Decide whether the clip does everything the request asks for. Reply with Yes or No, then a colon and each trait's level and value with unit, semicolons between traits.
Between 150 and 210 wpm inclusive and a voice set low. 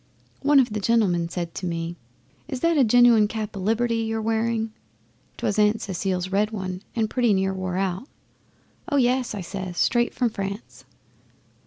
No: average, 170 wpm; high, 215 Hz